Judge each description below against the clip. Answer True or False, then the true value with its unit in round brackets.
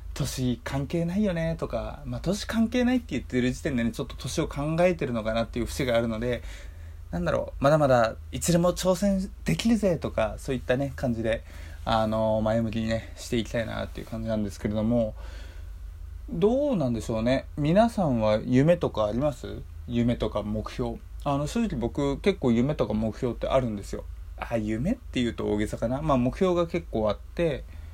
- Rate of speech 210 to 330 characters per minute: False (375 characters per minute)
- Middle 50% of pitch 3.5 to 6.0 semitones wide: True (5.2 semitones)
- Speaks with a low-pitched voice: True (115 Hz)